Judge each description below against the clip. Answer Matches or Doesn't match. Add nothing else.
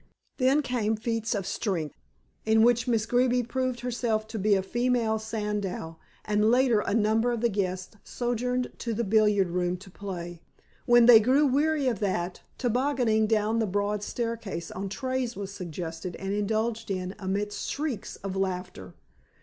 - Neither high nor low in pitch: Doesn't match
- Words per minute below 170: Matches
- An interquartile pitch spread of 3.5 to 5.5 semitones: Matches